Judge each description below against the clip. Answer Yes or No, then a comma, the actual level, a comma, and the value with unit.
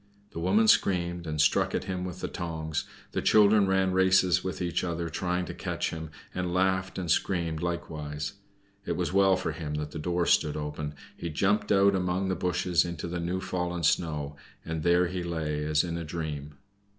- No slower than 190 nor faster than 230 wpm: Yes, average, 195 wpm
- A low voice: Yes, very low, 85 Hz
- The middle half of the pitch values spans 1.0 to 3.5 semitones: Yes, average, 2.8 semitones